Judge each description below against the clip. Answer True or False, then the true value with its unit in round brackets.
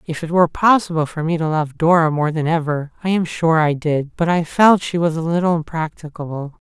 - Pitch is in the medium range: True (160 Hz)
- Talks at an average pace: False (225 wpm)